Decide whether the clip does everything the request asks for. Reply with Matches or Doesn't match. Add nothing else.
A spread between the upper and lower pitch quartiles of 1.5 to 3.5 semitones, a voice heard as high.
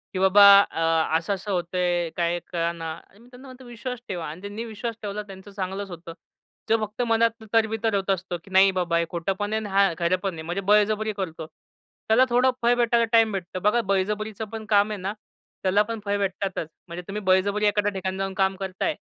Matches